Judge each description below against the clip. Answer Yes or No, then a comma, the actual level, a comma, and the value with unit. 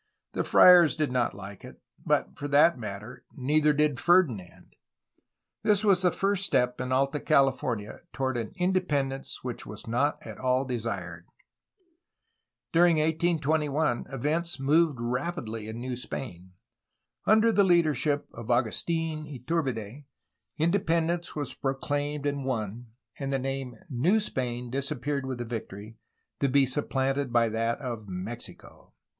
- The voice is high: No, low, 135 Hz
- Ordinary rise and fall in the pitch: Yes, average, 4.6 semitones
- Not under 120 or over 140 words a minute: Yes, slow, 135 wpm